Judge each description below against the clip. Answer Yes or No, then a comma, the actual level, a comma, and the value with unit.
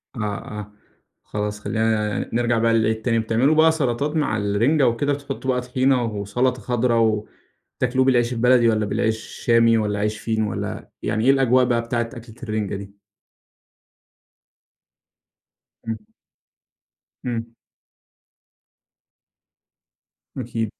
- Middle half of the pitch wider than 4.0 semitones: No, narrow, 2.6 semitones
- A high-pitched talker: No, low, 115 Hz